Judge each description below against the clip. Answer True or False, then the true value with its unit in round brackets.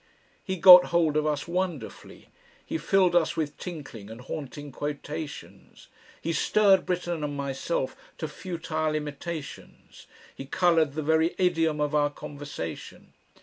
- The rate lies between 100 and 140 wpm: True (135 wpm)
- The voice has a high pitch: False (155 Hz)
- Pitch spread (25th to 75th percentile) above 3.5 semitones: False (3.0 semitones)